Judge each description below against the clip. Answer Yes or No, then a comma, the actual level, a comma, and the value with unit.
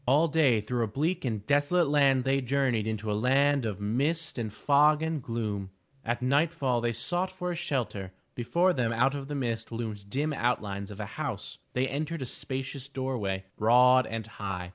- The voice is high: No, low, 125 Hz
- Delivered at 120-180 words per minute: No, average, 190 wpm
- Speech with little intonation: No, average, 4.5 semitones